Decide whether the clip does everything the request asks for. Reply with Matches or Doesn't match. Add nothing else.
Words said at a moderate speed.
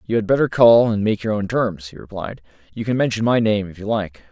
Doesn't match